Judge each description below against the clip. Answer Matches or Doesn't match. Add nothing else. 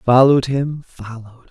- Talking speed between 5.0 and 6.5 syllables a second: Matches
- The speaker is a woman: Doesn't match